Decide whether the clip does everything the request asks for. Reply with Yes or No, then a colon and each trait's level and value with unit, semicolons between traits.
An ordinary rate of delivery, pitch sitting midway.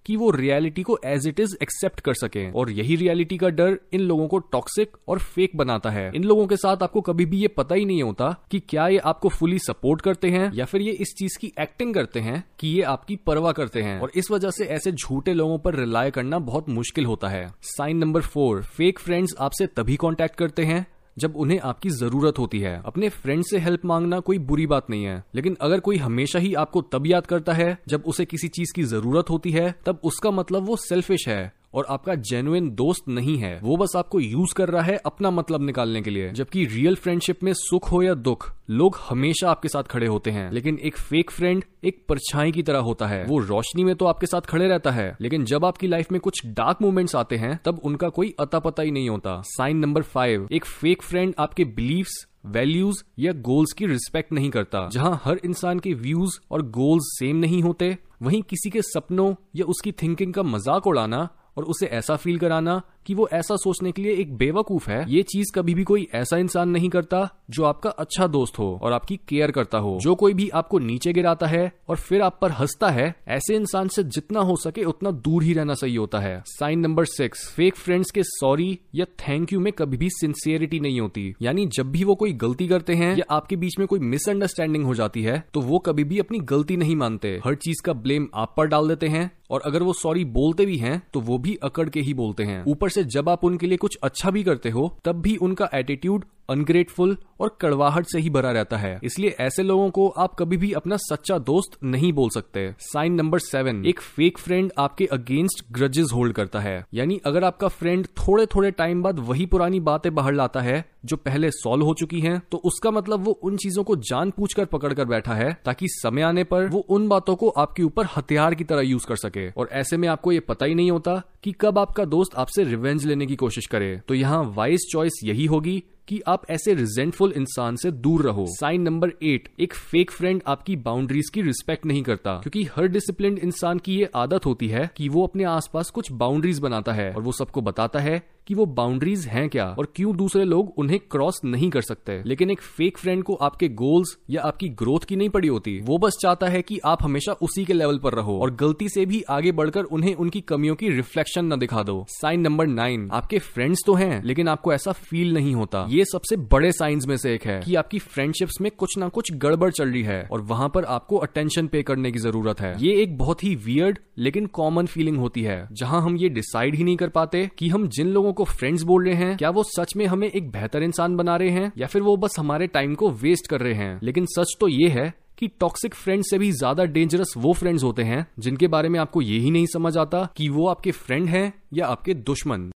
No: fast, 225 wpm; medium, 165 Hz